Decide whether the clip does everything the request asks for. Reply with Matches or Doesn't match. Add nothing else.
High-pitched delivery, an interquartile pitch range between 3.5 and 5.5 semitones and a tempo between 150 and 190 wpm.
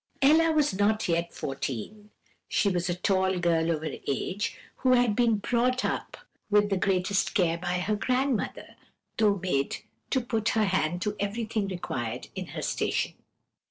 Matches